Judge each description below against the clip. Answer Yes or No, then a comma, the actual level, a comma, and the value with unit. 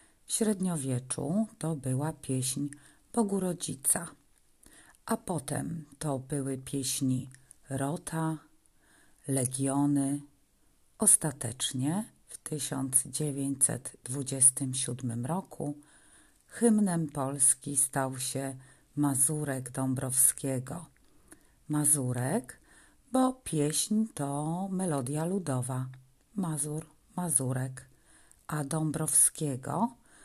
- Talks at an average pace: No, slow, 65 wpm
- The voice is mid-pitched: Yes, medium, 145 Hz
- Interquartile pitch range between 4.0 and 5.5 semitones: No, average, 3.2 semitones